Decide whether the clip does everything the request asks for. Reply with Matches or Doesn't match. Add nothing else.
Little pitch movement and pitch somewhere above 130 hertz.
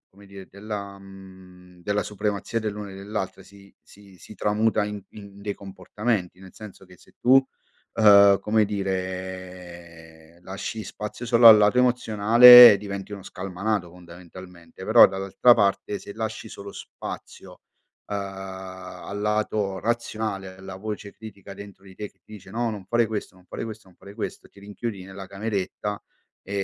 Doesn't match